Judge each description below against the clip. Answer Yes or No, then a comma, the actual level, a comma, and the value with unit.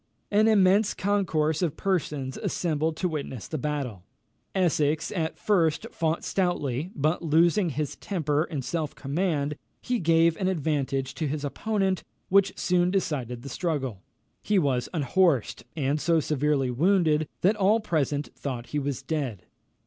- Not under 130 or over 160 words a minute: Yes, average, 145 wpm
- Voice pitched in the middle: Yes, medium, 155 Hz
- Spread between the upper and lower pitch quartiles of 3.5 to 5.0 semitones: Yes, average, 4.4 semitones